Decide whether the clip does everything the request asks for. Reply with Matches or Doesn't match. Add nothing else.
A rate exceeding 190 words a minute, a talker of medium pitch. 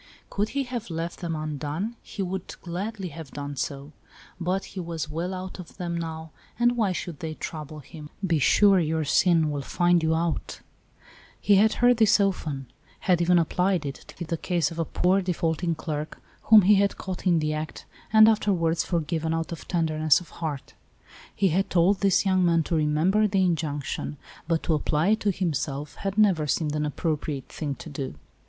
Matches